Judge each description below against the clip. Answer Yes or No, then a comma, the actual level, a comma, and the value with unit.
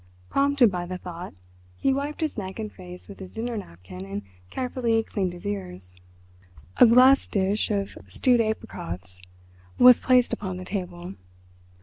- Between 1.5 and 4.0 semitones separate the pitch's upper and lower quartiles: No, wide, 5.5 semitones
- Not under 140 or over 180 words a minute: Yes, average, 150 wpm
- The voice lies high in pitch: Yes, high, 195 Hz